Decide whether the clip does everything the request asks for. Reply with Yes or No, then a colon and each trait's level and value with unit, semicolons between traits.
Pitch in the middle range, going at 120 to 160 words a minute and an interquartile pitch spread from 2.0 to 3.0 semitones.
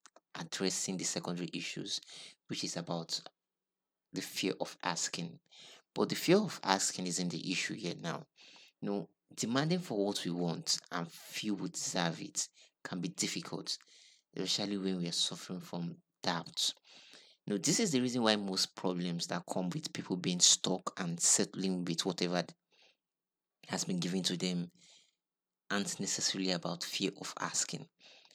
No: very low, 90 Hz; average, 155 wpm; narrow, 2.4 semitones